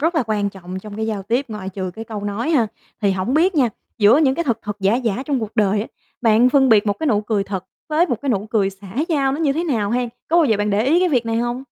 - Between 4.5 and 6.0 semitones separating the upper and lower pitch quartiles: Yes, average, 4.9 semitones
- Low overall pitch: No, high, 225 Hz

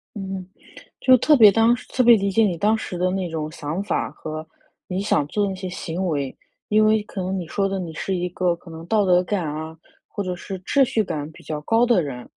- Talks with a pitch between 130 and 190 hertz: Yes, medium, 185 Hz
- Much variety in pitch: No, average, 4.3 semitones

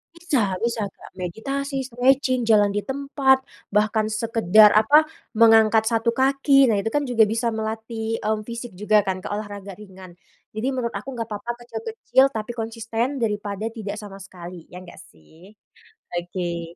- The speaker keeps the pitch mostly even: No, average, 3.0 semitones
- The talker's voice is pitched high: Yes, high, 220 Hz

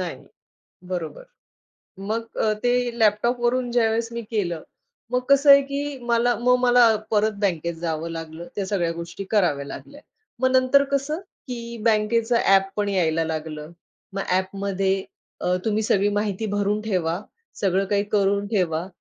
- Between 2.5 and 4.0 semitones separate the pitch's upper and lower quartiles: No, average, 4.6 semitones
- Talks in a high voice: Yes, high, 205 Hz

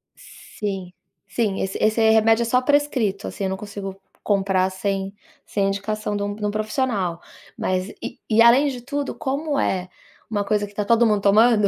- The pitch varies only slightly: No, average, 3.0 semitones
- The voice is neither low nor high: No, high, 210 Hz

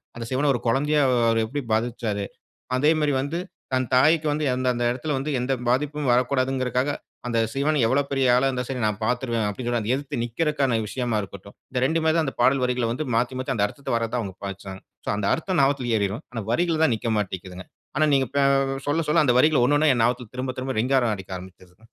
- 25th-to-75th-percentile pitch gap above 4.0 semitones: No, average, 3.7 semitones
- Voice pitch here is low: Yes, low, 125 Hz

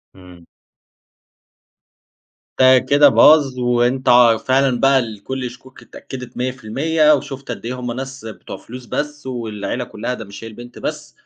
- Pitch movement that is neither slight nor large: No, narrow, 2.1 semitones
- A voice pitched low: Yes, low, 125 Hz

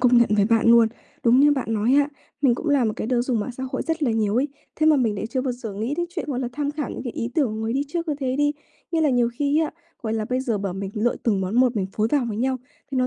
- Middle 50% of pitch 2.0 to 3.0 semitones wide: No, average, 4.2 semitones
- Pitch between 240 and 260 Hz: Yes, very high, 250 Hz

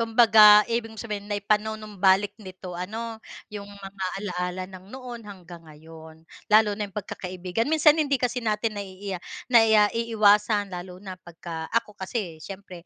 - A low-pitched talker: No, high, 205 Hz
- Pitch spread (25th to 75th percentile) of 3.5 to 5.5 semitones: No, average, 3.1 semitones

